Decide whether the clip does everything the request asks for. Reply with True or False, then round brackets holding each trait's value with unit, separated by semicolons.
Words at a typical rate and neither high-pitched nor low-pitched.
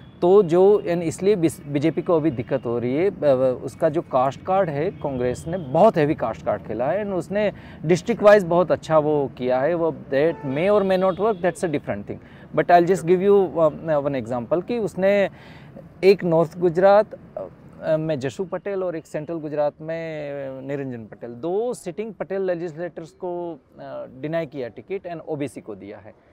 True (180 wpm; 170 Hz)